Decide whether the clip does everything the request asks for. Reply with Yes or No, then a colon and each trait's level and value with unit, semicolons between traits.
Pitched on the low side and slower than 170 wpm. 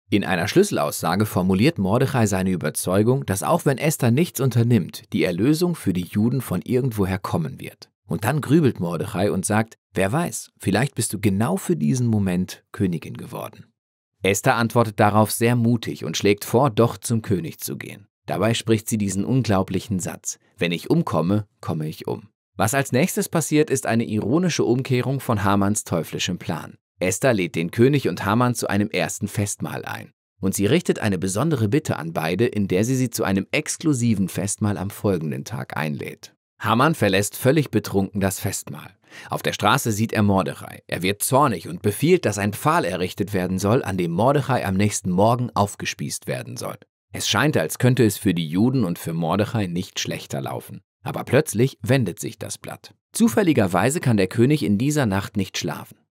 No: low, 110 Hz; average, 180 wpm